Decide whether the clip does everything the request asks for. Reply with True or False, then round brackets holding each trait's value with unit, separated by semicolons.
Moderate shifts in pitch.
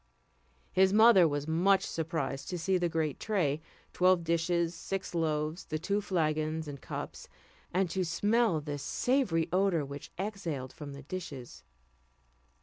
True (3.8 semitones)